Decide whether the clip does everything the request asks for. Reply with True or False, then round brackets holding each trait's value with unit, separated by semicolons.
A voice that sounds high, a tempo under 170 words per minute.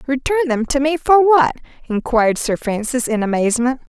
True (260 Hz; 150 wpm)